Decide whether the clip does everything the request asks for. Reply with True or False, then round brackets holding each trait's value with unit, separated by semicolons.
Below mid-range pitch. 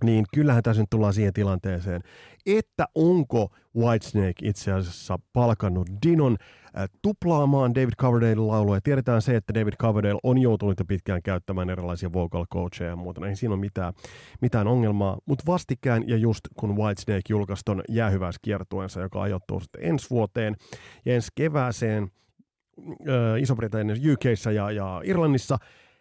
True (110 Hz)